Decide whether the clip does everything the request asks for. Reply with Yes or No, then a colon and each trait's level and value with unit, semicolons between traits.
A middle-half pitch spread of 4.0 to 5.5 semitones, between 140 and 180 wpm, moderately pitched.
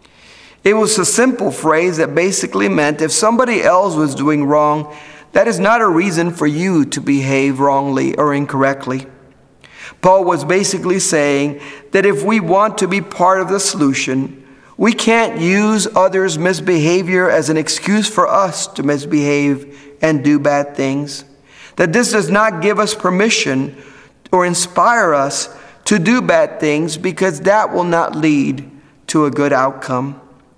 Yes: average, 5.1 semitones; average, 155 wpm; medium, 155 Hz